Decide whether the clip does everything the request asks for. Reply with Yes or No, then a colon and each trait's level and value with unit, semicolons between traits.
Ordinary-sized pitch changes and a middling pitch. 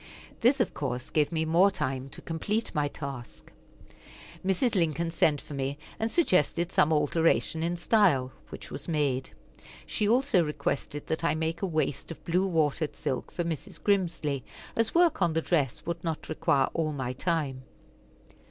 Yes: average, 3.7 semitones; medium, 160 Hz